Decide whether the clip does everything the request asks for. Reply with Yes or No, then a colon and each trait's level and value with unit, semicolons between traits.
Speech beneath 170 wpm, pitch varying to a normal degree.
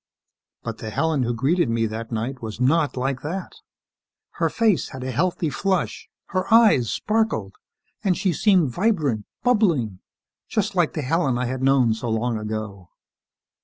No: average, 160 wpm; wide, 8.0 semitones